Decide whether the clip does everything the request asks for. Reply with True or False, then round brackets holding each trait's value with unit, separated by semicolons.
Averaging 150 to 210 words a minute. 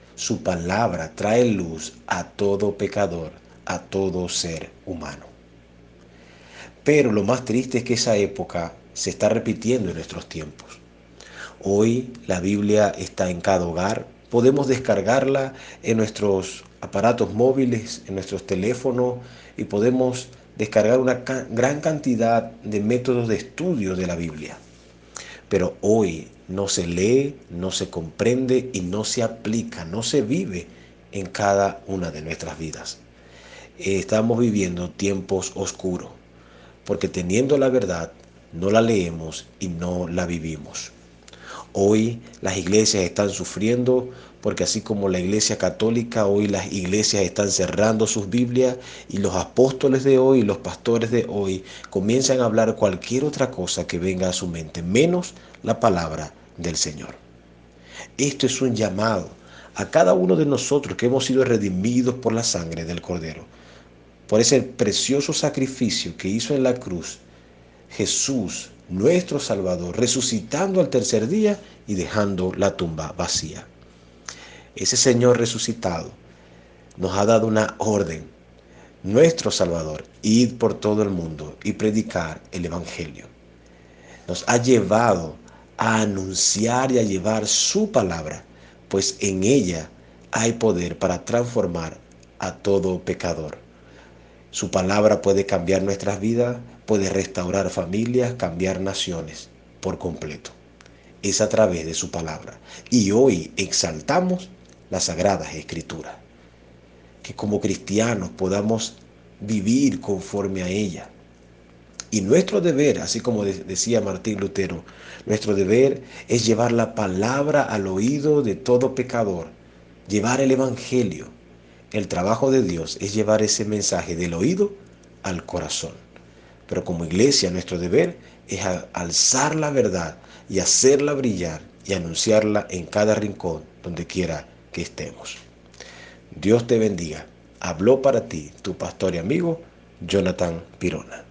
False (130 wpm)